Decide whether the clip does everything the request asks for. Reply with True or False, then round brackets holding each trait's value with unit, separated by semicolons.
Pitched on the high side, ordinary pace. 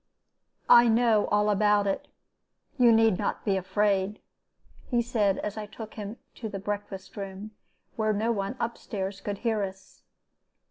True (210 Hz; 155 wpm)